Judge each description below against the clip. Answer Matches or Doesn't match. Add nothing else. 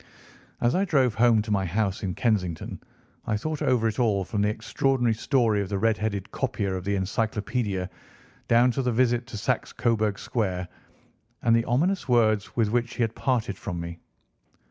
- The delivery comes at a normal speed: Matches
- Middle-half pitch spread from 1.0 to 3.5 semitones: Matches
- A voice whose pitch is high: Doesn't match